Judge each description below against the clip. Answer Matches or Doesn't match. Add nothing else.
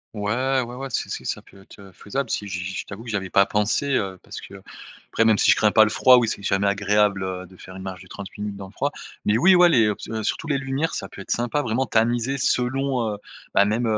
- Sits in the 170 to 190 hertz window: Doesn't match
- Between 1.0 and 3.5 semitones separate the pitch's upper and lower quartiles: Doesn't match